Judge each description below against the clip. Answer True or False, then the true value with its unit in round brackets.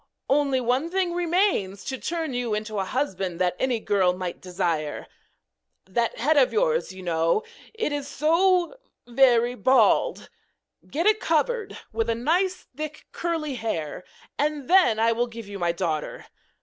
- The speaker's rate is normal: True (150 wpm)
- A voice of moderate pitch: False (255 Hz)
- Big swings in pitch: True (8.7 semitones)